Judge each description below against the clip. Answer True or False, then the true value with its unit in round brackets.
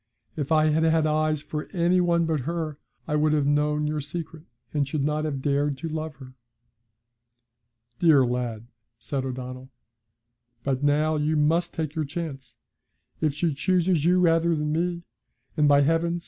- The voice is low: False (155 Hz)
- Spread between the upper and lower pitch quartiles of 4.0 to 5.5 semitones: False (2.4 semitones)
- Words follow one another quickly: False (165 wpm)